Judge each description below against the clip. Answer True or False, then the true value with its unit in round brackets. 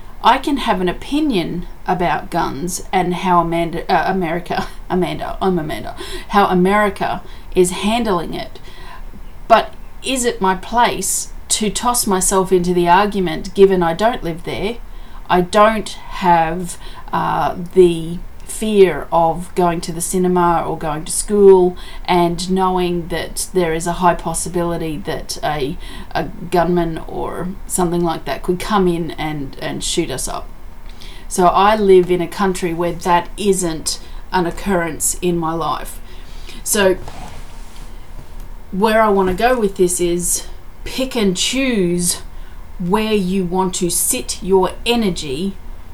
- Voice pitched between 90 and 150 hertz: False (180 Hz)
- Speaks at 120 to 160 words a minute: True (140 wpm)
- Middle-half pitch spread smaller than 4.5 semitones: True (2.4 semitones)